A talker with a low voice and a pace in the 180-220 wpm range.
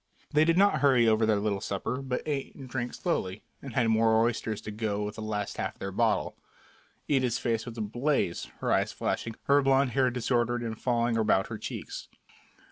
Yes: low, 120 Hz; average, 200 wpm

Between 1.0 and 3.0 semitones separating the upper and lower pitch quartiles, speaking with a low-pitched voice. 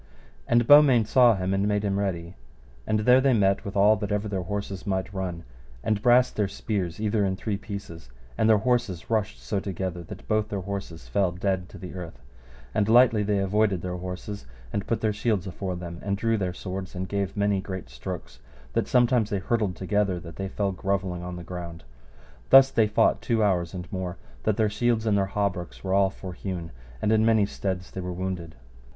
Yes: average, 2.7 semitones; low, 100 Hz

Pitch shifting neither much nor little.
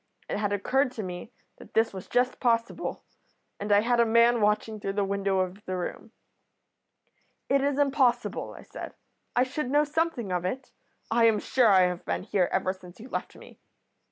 Yes: average, 4.3 semitones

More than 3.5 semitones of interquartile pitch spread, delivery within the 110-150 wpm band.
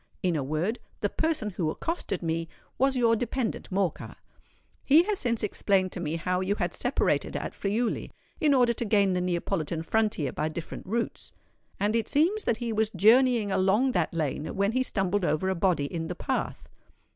No: average, 5.1 semitones; average, 185 wpm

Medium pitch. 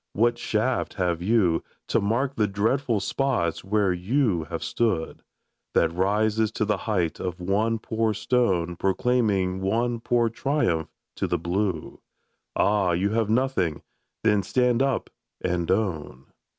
No: low, 105 Hz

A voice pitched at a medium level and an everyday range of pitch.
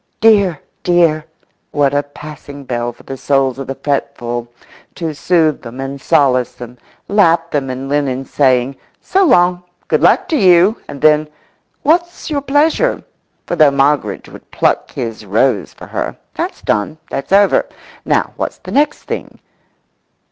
Yes: medium, 145 Hz; average, 4.9 semitones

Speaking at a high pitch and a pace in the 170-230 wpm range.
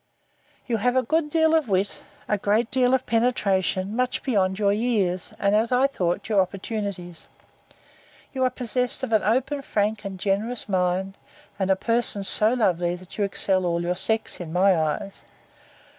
Yes: high, 205 Hz; average, 175 wpm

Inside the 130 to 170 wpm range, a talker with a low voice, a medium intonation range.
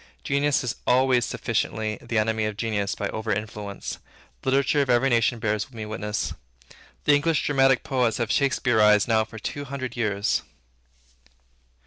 Yes: average, 150 wpm; low, 115 Hz; average, 3.7 semitones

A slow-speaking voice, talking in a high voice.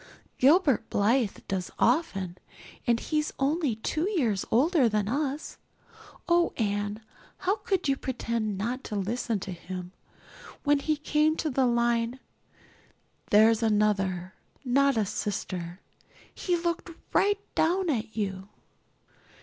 Yes: slow, 125 wpm; high, 235 Hz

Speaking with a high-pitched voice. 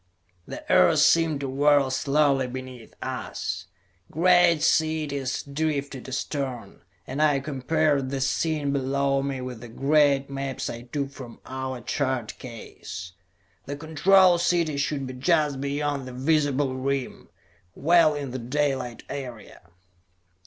No: medium, 140 Hz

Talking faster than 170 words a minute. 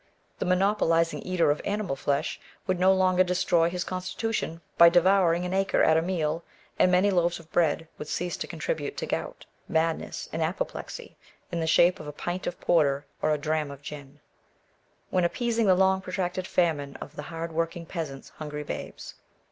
Yes: average, 180 wpm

